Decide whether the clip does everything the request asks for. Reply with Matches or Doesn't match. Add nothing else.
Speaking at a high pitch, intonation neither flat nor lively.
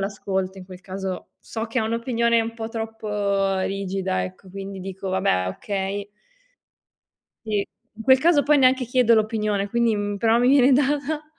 Matches